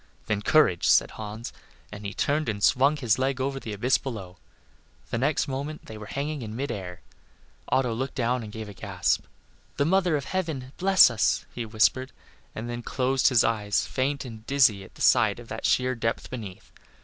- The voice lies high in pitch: No, low, 125 Hz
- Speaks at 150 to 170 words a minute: No, average, 195 wpm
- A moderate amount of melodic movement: Yes, average, 4.2 semitones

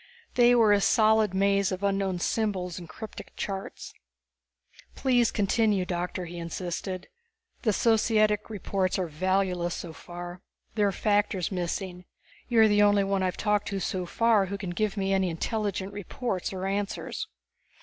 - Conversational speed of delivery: Yes, average, 160 wpm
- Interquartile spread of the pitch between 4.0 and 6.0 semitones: No, narrow, 2.6 semitones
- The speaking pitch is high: Yes, high, 195 Hz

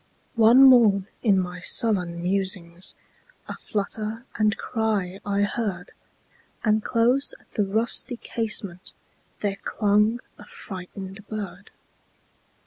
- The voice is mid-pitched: No, high, 205 Hz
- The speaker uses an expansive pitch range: No, average, 2.9 semitones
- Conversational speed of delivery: No, slow, 95 wpm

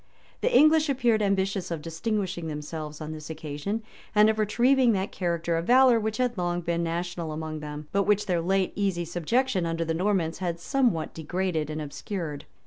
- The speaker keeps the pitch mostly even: No, average, 4.6 semitones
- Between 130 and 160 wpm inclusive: No, average, 185 wpm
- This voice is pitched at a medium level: Yes, medium, 175 Hz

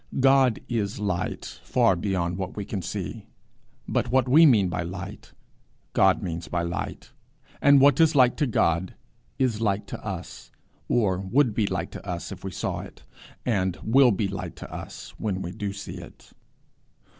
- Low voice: Yes, low, 100 Hz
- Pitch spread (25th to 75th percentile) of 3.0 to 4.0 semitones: No, average, 4.9 semitones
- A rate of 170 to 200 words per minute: Yes, average, 175 wpm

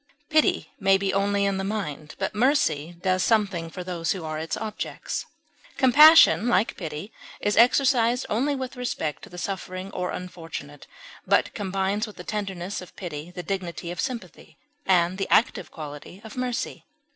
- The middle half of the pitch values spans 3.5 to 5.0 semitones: Yes, average, 4.1 semitones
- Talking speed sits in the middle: Yes, average, 165 wpm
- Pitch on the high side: Yes, high, 195 Hz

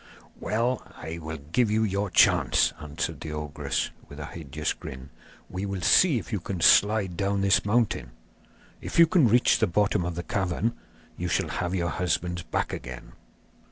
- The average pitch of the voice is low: Yes, very low, 90 Hz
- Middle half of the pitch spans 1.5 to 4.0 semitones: No, average, 4.6 semitones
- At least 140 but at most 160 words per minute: No, average, 175 wpm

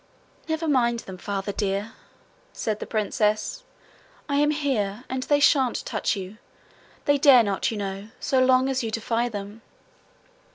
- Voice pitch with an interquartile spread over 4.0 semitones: Yes, average, 4.7 semitones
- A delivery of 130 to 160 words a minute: Yes, average, 155 wpm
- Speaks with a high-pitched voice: Yes, high, 230 Hz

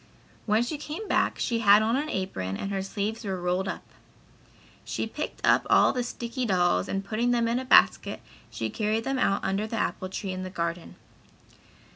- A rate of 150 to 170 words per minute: No, average, 195 wpm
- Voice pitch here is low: No, high, 210 Hz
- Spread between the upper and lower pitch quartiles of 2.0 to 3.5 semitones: No, average, 4.0 semitones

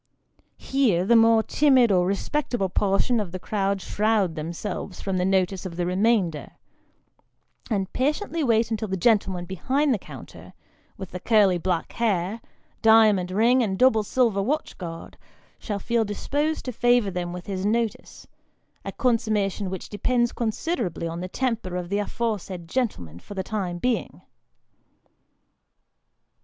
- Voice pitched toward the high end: Yes, high, 205 Hz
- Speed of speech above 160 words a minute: No, average, 150 wpm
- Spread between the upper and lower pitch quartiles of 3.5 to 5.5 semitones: Yes, average, 4.2 semitones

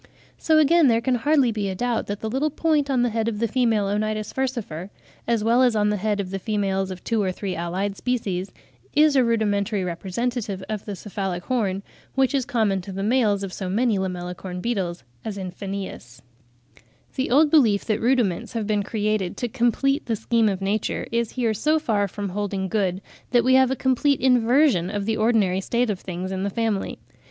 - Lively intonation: No, average, 4.0 semitones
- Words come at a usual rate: No, fast, 210 wpm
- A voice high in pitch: Yes, high, 215 Hz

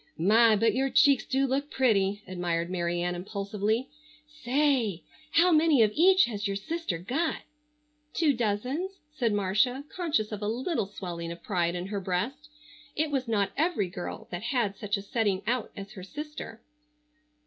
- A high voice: Yes, high, 220 Hz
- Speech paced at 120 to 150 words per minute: No, average, 165 wpm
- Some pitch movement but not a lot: No, wide, 6.0 semitones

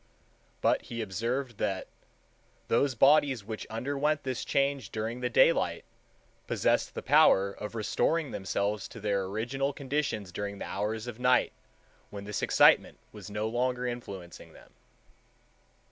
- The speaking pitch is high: No, low, 115 Hz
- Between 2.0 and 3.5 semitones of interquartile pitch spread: No, average, 4.3 semitones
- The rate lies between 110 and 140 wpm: Yes, slow, 135 wpm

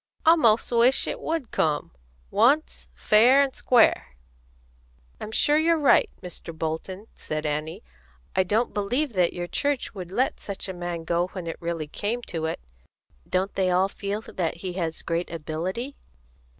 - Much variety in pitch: Yes, wide, 6.1 semitones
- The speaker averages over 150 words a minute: Yes, average, 165 wpm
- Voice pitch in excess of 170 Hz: Yes, high, 190 Hz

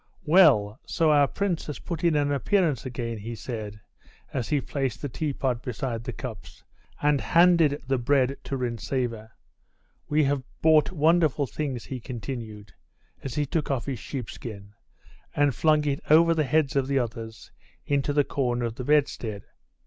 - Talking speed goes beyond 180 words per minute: No, average, 165 wpm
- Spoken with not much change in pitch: No, average, 4.2 semitones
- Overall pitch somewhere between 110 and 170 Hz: Yes, low, 135 Hz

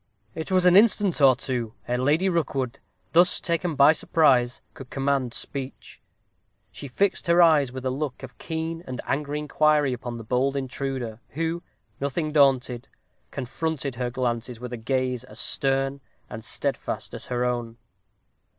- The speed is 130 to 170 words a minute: Yes, average, 155 wpm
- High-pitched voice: No, low, 135 Hz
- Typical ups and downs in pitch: Yes, average, 3.8 semitones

